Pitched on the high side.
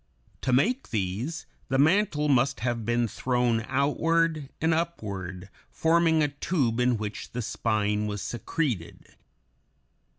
No: low, 125 Hz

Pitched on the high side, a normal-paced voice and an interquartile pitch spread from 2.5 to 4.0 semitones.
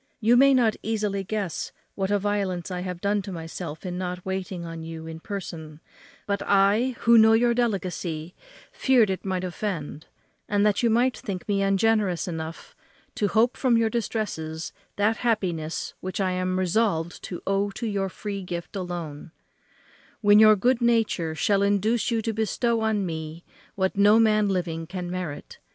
Yes: high, 195 Hz; average, 170 wpm; average, 3.6 semitones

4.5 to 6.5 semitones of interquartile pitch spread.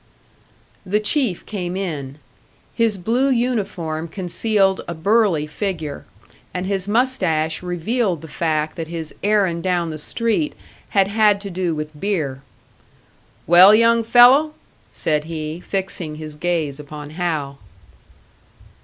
Yes: average, 5.1 semitones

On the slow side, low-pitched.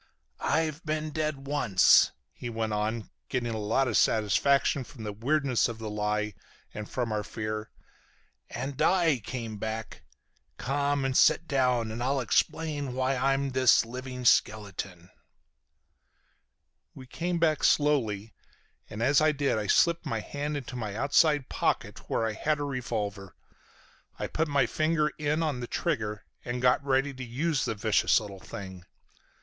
No: average, 155 wpm; low, 125 Hz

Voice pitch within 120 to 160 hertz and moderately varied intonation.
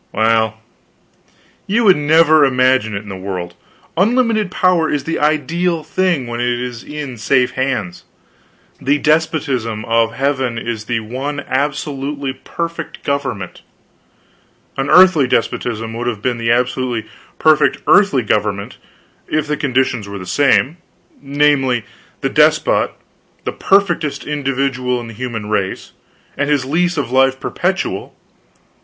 Yes: low, 135 Hz; average, 4.5 semitones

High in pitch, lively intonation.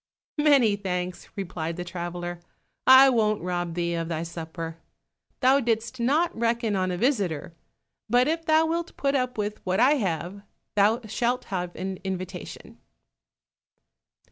Yes: high, 200 Hz; wide, 6.2 semitones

